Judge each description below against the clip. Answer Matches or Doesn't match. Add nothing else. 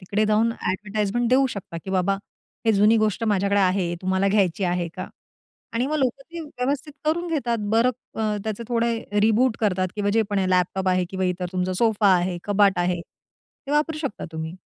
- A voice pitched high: Matches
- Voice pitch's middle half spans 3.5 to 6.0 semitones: Matches